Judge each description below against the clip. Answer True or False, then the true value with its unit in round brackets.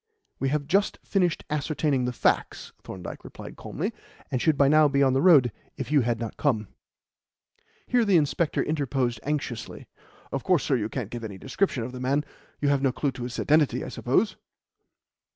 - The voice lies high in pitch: False (140 Hz)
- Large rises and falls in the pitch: False (3.5 semitones)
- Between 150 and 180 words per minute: False (190 wpm)